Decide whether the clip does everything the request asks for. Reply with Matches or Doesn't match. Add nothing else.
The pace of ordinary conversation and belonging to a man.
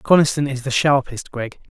Matches